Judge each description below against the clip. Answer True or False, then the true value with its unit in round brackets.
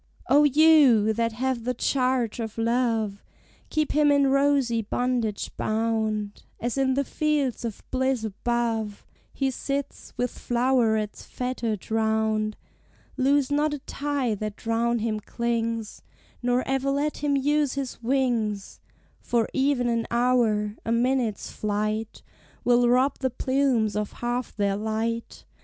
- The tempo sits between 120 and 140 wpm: True (135 wpm)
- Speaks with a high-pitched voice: True (240 Hz)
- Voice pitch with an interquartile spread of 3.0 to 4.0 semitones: True (3.3 semitones)